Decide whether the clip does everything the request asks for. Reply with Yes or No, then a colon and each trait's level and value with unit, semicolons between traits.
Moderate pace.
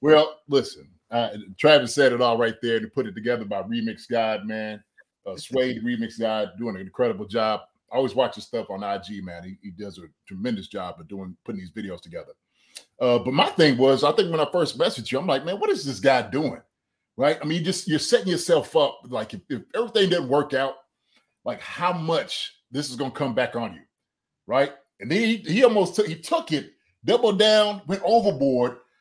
No: fast, 215 wpm